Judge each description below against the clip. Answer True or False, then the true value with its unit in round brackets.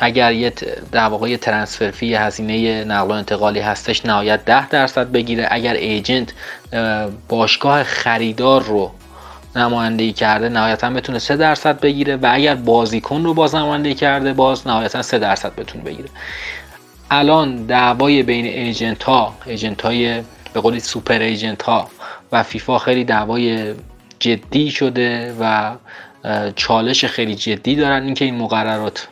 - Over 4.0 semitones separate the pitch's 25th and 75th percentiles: False (3.1 semitones)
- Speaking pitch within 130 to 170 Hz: False (115 Hz)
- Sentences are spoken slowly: False (135 wpm)